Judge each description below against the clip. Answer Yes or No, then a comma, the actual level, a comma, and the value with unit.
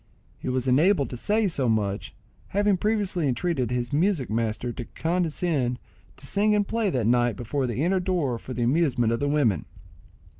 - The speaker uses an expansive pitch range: Yes, wide, 6.9 semitones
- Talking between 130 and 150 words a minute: No, average, 180 wpm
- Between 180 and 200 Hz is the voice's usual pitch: No, medium, 140 Hz